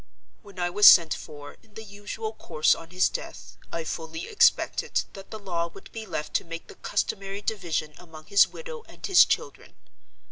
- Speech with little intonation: No, average, 4.1 semitones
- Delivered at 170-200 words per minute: Yes, average, 185 wpm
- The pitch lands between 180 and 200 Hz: Yes, medium, 185 Hz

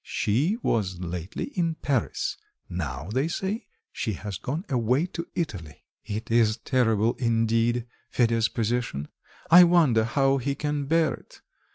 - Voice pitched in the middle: No, low, 120 Hz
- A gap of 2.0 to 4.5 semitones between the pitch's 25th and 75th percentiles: No, average, 5.3 semitones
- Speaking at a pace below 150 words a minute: Yes, average, 140 wpm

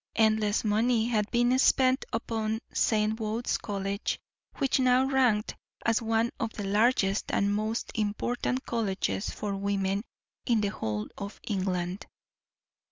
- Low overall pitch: No, high, 215 Hz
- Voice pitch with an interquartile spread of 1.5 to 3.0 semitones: Yes, average, 2.7 semitones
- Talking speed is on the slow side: Yes, slow, 130 wpm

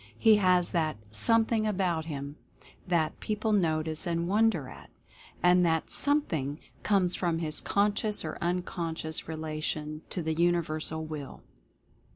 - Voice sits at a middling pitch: Yes, medium, 170 Hz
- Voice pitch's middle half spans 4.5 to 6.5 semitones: No, average, 3.8 semitones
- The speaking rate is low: Yes, slow, 130 wpm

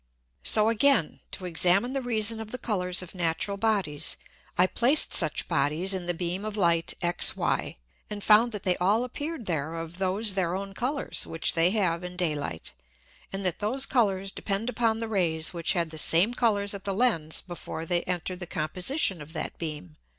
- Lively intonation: No, average, 4.5 semitones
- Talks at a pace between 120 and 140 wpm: No, average, 190 wpm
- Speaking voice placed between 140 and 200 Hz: Yes, high, 190 Hz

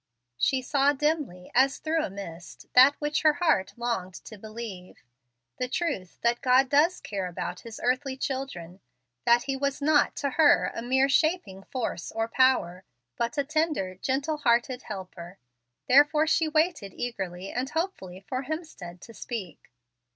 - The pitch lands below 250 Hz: No, very high, 255 Hz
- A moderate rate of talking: Yes, average, 155 wpm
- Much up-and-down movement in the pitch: Yes, wide, 7.1 semitones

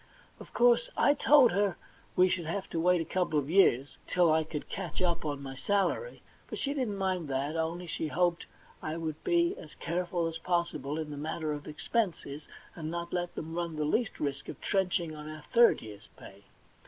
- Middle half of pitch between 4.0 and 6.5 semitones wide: No, average, 3.4 semitones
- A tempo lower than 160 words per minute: No, fast, 205 wpm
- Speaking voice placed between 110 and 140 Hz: No, medium, 170 Hz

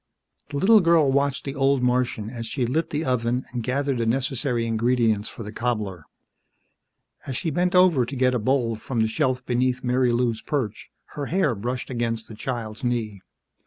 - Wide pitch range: No, average, 3.0 semitones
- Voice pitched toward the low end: Yes, low, 125 Hz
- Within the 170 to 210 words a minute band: Yes, average, 180 wpm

